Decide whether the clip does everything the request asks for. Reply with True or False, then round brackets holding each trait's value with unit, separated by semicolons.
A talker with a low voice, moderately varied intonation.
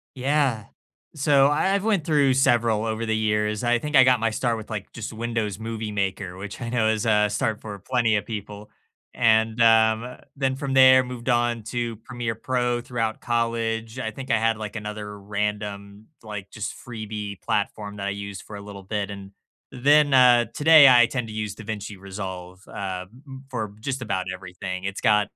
True (110 Hz; 3.0 semitones)